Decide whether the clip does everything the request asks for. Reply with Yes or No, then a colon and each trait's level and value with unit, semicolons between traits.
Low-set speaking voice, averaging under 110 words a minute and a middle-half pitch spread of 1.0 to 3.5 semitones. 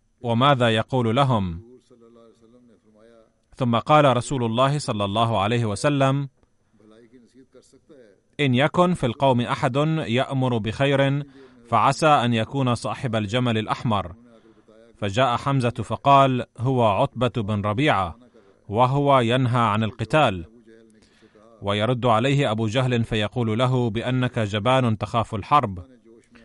Yes: low, 120 Hz; average, 100 wpm; average, 3.1 semitones